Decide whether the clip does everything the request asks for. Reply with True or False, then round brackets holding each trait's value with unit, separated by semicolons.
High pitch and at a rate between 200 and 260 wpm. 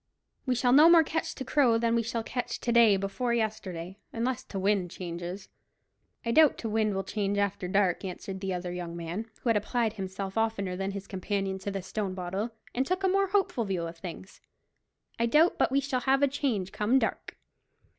True (210 Hz; 205 wpm)